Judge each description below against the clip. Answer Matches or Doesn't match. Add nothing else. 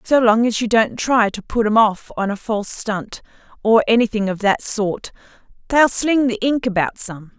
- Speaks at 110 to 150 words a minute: Doesn't match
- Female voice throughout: Matches